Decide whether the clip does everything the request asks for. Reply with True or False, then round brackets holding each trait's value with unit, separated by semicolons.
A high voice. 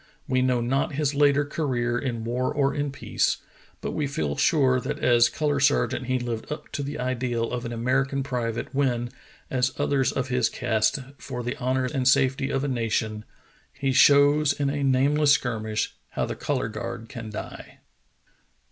False (130 Hz)